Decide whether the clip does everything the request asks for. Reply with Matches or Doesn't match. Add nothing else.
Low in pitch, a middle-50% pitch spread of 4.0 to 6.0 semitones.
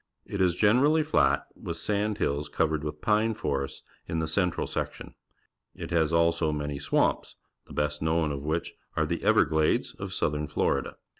Matches